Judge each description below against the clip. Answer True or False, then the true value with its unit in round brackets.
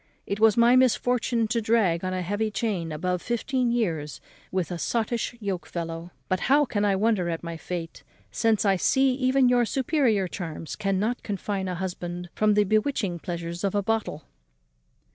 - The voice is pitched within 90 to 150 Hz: False (205 Hz)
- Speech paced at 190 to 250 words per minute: False (175 wpm)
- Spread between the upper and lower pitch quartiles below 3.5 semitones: False (4.8 semitones)